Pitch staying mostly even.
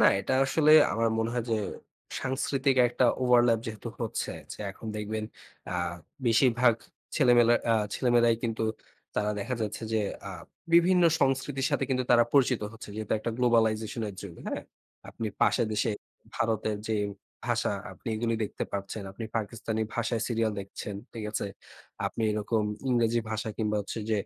Yes: narrow, 2.1 semitones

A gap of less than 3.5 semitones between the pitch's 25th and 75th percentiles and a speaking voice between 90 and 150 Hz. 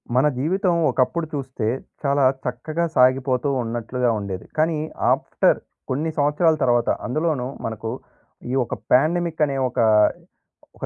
No: average, 4.1 semitones; low, 135 Hz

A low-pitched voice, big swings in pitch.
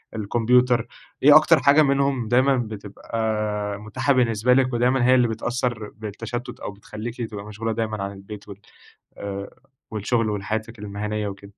No: low, 110 Hz; average, 3.0 semitones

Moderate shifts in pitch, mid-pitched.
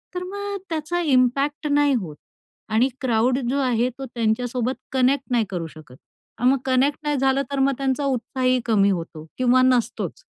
No: average, 3.0 semitones; very high, 255 Hz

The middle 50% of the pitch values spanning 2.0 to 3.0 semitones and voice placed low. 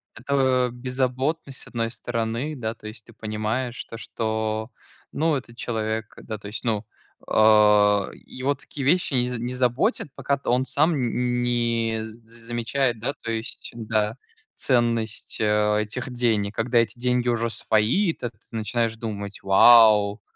Yes: narrow, 2.4 semitones; low, 115 Hz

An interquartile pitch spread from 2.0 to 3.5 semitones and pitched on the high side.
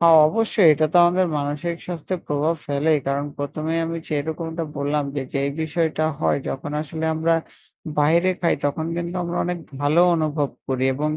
No: average, 2.7 semitones; medium, 160 Hz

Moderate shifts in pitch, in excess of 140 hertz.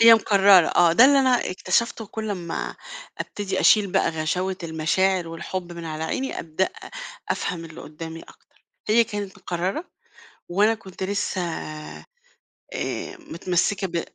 Yes: average, 3.6 semitones; high, 190 Hz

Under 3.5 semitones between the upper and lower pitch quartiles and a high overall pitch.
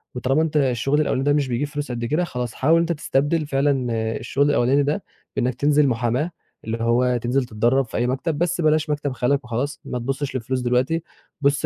No: average, 3.1 semitones; low, 135 Hz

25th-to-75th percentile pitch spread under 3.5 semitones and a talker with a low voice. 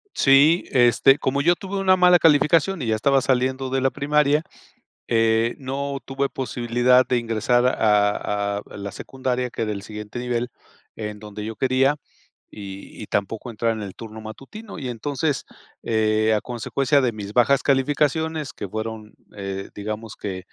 No: average, 4.3 semitones; low, 125 Hz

